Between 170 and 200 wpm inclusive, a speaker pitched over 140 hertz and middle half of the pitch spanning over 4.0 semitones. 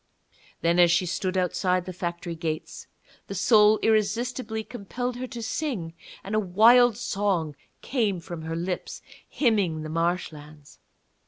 No: average, 140 wpm; high, 190 Hz; average, 4.6 semitones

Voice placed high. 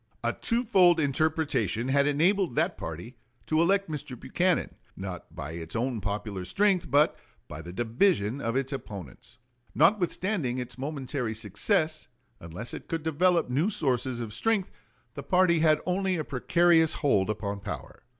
No: medium, 140 Hz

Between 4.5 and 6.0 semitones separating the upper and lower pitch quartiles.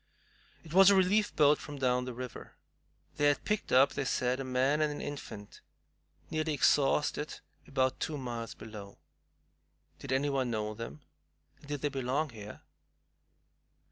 No: average, 3.0 semitones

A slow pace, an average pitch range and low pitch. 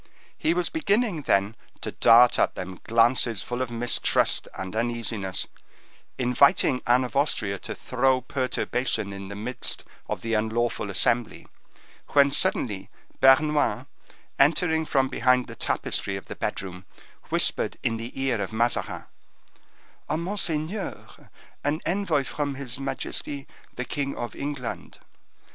Yes: slow, 130 wpm; average, 3.9 semitones; low, 125 Hz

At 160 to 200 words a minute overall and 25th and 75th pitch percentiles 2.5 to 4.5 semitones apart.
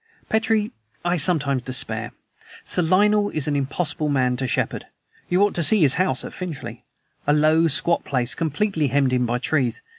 No: average, 175 wpm; average, 5.1 semitones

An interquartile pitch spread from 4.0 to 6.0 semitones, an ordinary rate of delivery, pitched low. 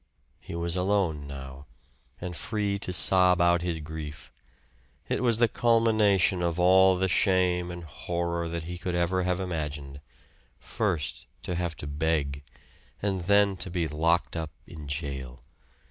No: average, 3.1 semitones; average, 150 wpm; very low, 85 Hz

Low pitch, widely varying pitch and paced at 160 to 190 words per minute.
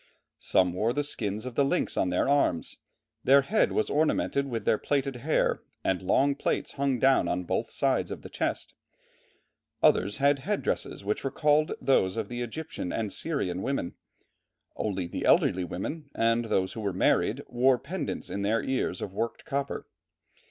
Yes: low, 120 Hz; wide, 6.1 semitones; average, 170 wpm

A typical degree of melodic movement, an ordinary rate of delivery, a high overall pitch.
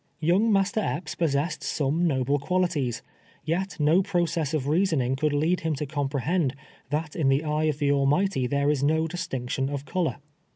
No: average, 3.5 semitones; average, 175 wpm; medium, 150 Hz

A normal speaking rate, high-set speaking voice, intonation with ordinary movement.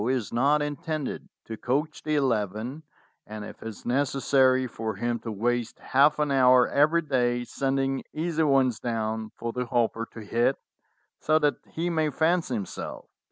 No: average, 160 wpm; low, 130 Hz; average, 4.0 semitones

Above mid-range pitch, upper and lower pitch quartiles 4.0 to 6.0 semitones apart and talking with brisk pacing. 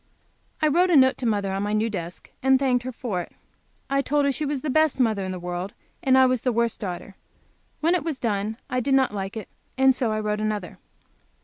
Yes: high, 240 Hz; average, 4.6 semitones; fast, 245 wpm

